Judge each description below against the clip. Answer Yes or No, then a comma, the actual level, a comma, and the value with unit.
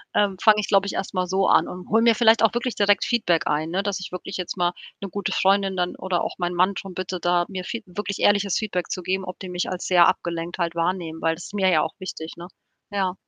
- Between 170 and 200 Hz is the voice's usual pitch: Yes, medium, 185 Hz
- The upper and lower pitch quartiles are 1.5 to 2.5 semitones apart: Yes, narrow, 2.2 semitones